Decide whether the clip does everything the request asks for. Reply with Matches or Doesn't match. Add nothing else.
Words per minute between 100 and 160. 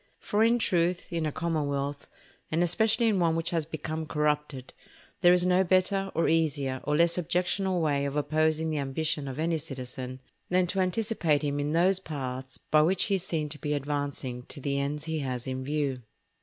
Doesn't match